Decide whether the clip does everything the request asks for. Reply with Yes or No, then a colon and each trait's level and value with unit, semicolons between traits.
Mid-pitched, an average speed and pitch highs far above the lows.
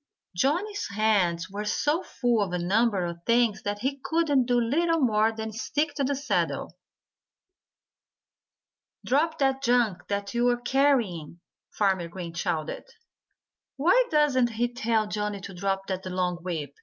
No: high, 220 Hz; average, 145 wpm; wide, 6.0 semitones